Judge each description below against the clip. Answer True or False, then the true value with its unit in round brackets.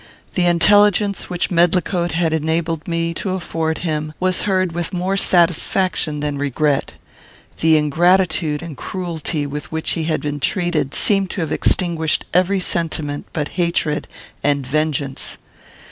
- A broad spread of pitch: False (2.9 semitones)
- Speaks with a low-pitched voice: False (165 Hz)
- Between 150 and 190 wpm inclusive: False (140 wpm)